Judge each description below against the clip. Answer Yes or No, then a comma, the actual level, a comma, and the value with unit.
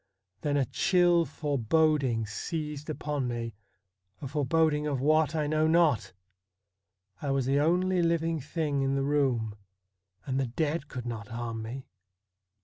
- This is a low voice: No, medium, 145 Hz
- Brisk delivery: No, average, 145 wpm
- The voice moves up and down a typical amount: Yes, average, 4.1 semitones